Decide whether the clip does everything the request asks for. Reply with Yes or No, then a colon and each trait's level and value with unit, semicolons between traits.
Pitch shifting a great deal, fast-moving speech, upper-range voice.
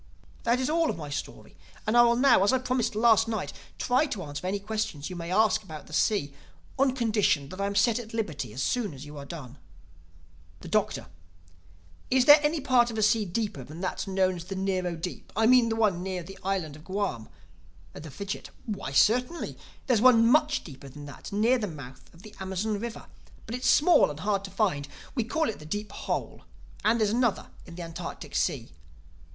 Yes: wide, 5.8 semitones; fast, 210 wpm; high, 205 Hz